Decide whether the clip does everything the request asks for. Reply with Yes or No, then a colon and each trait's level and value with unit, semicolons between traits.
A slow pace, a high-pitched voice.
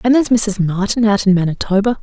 No: fast, 205 wpm; high, 210 Hz